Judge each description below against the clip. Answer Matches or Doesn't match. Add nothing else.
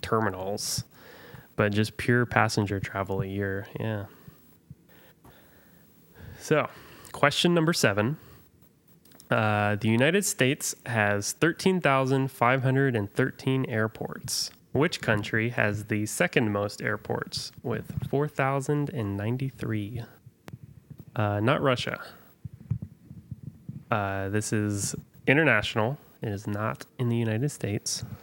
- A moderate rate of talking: Doesn't match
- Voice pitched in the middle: Doesn't match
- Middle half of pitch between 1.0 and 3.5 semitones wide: Doesn't match